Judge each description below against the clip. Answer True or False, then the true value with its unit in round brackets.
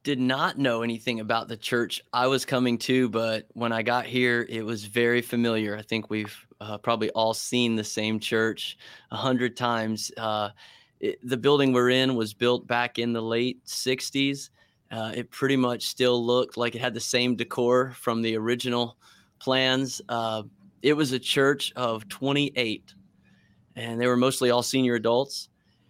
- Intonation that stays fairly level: True (2.2 semitones)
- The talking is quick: False (175 wpm)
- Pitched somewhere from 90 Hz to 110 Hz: False (120 Hz)